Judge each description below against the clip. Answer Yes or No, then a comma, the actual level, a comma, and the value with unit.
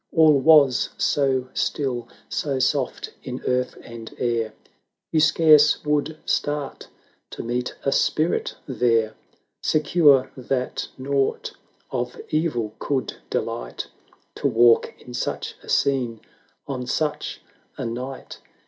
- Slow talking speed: Yes, slow, 115 wpm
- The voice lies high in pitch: No, low, 130 Hz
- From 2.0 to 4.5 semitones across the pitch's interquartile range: Yes, average, 3.2 semitones